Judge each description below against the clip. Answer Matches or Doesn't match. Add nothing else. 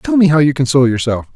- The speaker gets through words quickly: Matches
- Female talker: Doesn't match